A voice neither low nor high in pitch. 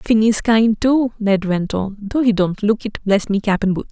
No: high, 210 Hz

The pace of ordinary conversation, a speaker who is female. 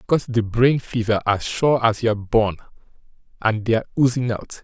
No: average, 180 wpm; male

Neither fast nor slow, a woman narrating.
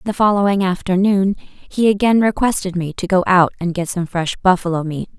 Yes: average, 185 wpm; female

